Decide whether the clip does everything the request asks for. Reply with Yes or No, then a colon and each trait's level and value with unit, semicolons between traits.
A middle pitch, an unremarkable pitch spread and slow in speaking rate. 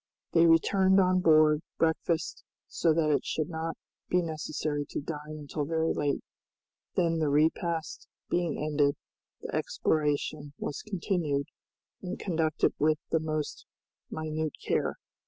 No: medium, 160 Hz; narrow, 1.8 semitones; slow, 130 wpm